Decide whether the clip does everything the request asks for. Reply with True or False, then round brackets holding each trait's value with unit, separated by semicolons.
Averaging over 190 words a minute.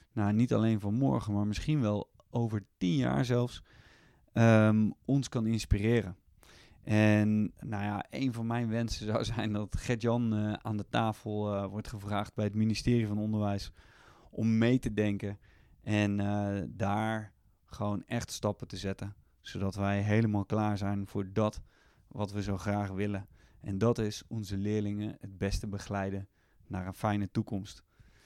False (155 wpm)